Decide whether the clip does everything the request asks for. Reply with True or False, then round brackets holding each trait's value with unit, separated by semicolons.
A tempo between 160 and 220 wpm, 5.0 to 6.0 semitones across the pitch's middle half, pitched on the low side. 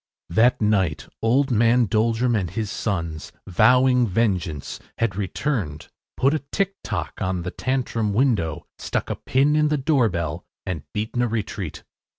False (145 wpm; 5.4 semitones; 110 Hz)